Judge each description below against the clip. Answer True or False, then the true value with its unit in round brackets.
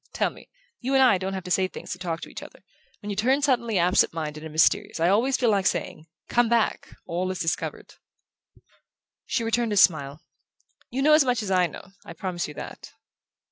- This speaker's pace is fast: True (210 wpm)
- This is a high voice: True (195 Hz)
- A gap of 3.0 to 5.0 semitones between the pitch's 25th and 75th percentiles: False (5.5 semitones)